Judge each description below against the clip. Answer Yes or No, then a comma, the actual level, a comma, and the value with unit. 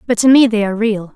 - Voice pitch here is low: No, high, 220 Hz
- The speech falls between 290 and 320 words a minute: Yes, fast, 310 wpm